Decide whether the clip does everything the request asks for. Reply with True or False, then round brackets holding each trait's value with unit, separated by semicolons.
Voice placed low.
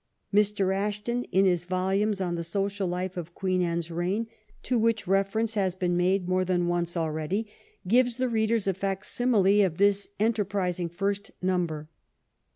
False (190 Hz)